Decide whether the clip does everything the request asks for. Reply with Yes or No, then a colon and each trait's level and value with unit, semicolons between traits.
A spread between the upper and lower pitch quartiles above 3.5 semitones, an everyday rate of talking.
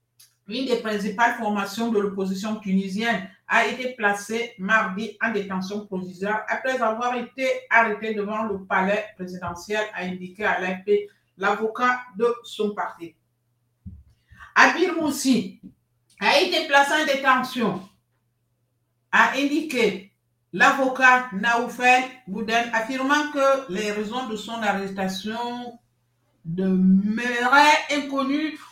No: average, 4.5 semitones; slow, 105 wpm